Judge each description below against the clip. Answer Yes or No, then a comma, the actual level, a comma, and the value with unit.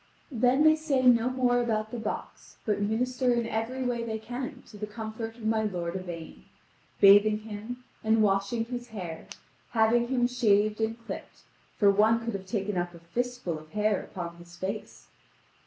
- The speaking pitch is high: Yes, high, 220 Hz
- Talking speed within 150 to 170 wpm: No, average, 180 wpm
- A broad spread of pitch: No, average, 3.3 semitones